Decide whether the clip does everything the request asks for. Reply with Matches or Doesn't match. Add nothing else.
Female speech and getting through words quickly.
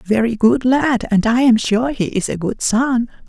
Doesn't match